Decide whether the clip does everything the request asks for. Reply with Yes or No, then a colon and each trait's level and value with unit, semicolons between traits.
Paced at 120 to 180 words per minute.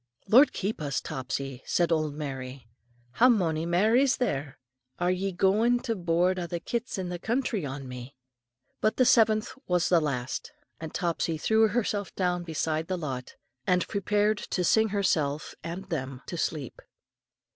Yes: average, 165 wpm